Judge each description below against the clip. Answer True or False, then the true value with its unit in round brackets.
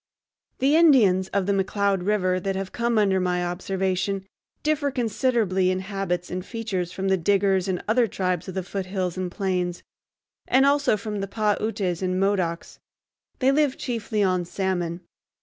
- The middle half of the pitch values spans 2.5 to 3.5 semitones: True (2.8 semitones)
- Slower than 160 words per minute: False (165 wpm)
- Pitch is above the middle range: True (195 Hz)